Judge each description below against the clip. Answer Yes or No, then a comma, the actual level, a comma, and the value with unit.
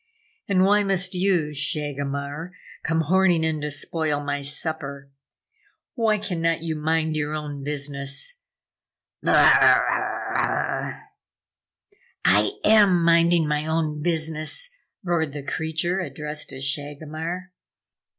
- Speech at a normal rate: No, slow, 110 wpm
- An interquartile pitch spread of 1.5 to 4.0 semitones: Yes, average, 3.0 semitones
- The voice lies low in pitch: No, medium, 160 Hz